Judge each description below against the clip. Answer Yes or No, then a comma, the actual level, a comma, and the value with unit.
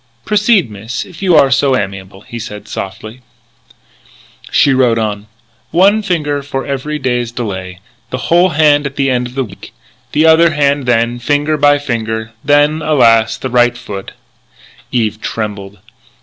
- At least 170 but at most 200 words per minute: No, average, 155 wpm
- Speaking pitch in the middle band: No, low, 130 Hz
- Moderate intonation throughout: Yes, average, 4.8 semitones